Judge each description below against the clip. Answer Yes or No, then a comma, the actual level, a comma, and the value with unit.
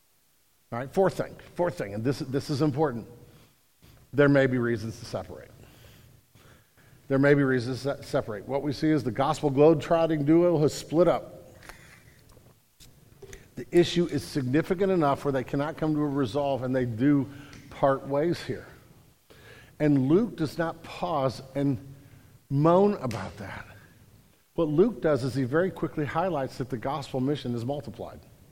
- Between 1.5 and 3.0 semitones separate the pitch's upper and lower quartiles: No, average, 3.5 semitones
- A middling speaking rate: Yes, average, 160 wpm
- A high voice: No, medium, 140 Hz